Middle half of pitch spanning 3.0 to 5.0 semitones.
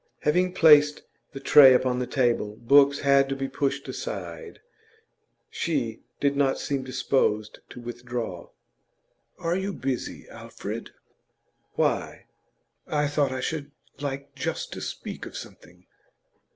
No: narrow, 2.6 semitones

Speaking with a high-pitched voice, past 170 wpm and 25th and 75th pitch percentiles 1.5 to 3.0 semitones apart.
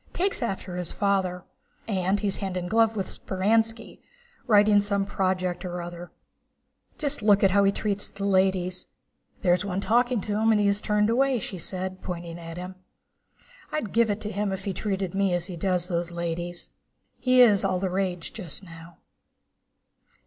Yes: high, 195 Hz; average, 180 wpm; narrow, 2.6 semitones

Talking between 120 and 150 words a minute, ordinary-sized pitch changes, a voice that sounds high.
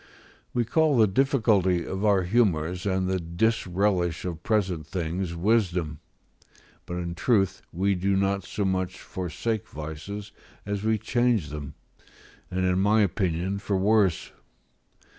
No: slow, 135 wpm; average, 3.2 semitones; very low, 95 Hz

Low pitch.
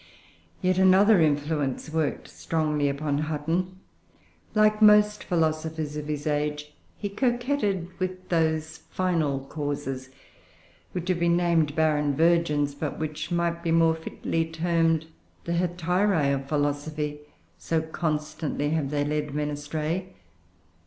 No: medium, 160 Hz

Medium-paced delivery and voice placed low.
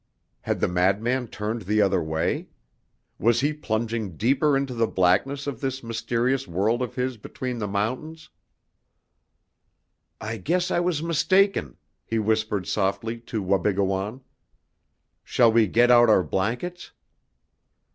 No: slow, 130 wpm; low, 115 Hz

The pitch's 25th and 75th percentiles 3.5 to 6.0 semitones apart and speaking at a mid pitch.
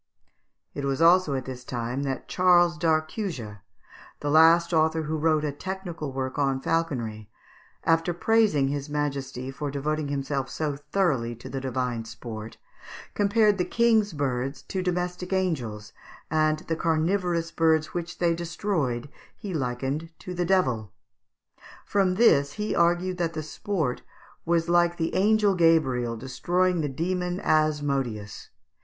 Yes: average, 4.7 semitones; medium, 155 Hz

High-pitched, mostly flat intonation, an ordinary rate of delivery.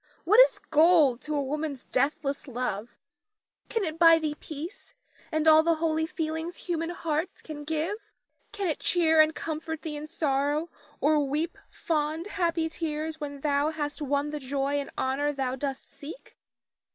Yes: very high, 310 Hz; narrow, 2.2 semitones; average, 165 wpm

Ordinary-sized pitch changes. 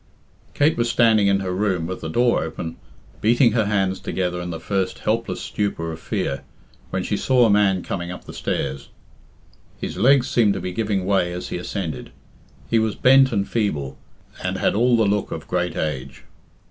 Yes: average, 4.3 semitones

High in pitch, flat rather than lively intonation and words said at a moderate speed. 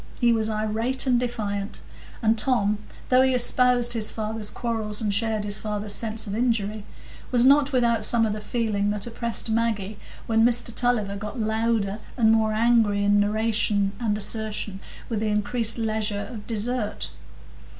Yes: high, 220 Hz; narrow, 2.0 semitones; average, 160 wpm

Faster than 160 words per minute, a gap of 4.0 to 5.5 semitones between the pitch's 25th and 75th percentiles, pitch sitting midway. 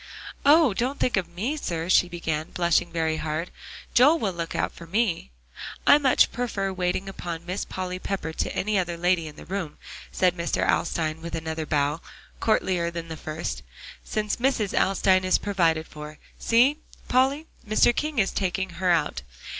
Yes: average, 170 wpm; average, 4.3 semitones; medium, 180 Hz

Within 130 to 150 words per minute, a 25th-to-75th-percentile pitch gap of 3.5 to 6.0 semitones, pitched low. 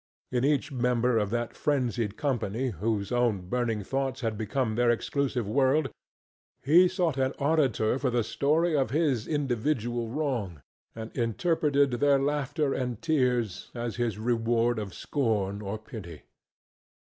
Yes: average, 140 wpm; average, 4.0 semitones; low, 120 Hz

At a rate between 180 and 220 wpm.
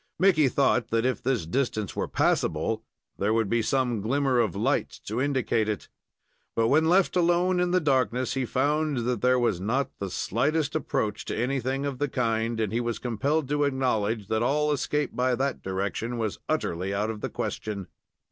Yes: average, 185 wpm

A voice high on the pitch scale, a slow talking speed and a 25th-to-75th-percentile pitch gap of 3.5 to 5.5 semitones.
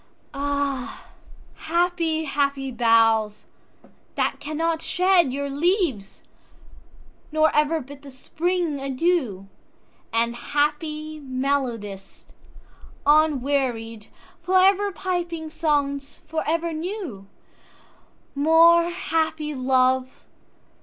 Yes: very high, 295 Hz; slow, 70 wpm; average, 4.2 semitones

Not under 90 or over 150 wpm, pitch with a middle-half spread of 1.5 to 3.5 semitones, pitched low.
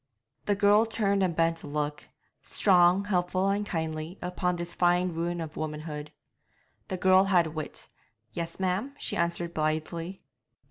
No: average, 145 wpm; average, 2.8 semitones; medium, 175 Hz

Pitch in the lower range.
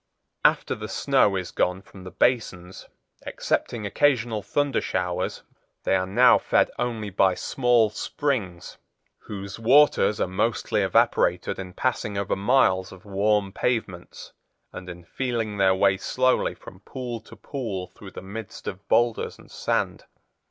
Yes: low, 100 Hz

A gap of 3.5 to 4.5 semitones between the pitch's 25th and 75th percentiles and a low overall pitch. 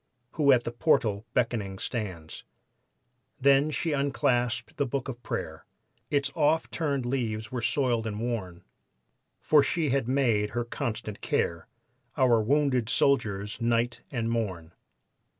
Yes: average, 4.1 semitones; low, 120 Hz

